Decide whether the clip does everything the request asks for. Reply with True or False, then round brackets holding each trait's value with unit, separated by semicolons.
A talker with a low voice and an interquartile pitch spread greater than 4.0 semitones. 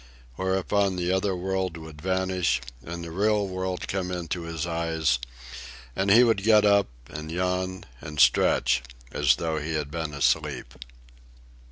False (90 Hz; 3.1 semitones)